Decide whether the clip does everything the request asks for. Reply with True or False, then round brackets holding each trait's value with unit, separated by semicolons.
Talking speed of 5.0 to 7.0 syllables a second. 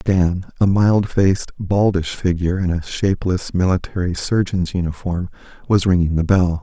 False (4.8 syllables/s)